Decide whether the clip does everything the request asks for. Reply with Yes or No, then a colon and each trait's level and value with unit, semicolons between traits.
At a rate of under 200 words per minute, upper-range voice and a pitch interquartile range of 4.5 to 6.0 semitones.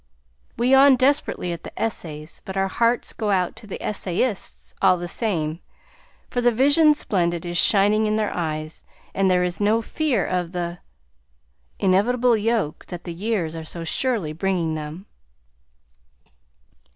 Yes: average, 150 wpm; high, 195 Hz; average, 5.0 semitones